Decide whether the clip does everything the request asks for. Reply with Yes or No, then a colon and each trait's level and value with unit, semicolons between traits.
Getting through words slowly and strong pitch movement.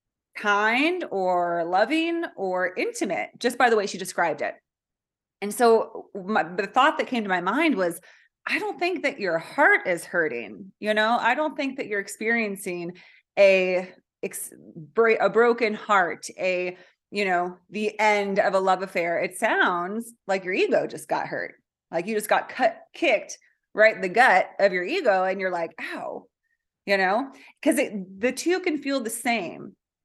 No: average, 170 wpm; wide, 6.5 semitones